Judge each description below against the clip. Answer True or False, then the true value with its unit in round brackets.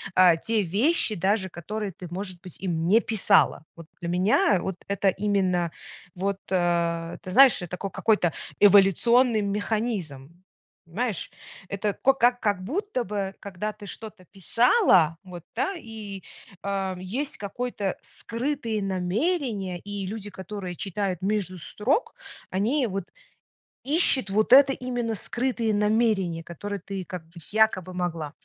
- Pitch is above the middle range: True (200 Hz)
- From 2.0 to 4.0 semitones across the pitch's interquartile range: True (3.5 semitones)